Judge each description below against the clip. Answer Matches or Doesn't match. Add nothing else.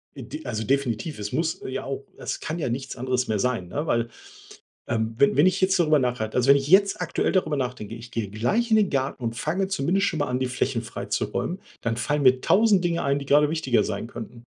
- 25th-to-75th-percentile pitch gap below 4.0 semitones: Doesn't match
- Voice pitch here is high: Doesn't match